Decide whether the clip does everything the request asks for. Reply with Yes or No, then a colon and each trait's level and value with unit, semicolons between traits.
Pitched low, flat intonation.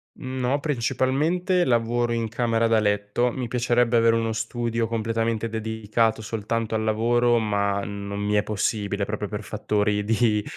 Yes: low, 115 Hz; narrow, 2.2 semitones